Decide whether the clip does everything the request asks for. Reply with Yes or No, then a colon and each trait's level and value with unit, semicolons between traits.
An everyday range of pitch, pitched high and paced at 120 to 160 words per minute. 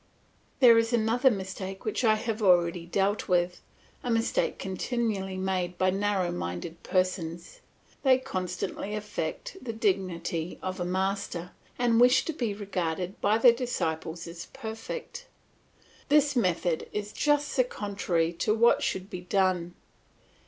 Yes: average, 4.2 semitones; high, 195 Hz; average, 140 wpm